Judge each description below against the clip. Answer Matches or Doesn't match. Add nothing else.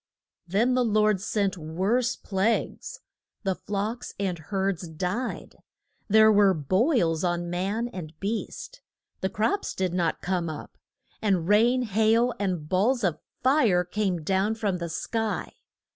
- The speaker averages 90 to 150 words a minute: Matches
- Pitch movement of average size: Matches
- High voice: Matches